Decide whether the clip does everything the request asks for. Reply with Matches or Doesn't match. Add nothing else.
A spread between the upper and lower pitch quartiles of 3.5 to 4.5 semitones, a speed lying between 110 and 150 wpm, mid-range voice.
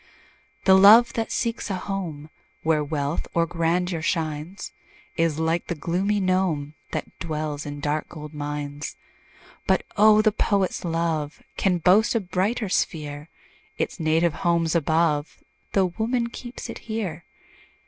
Matches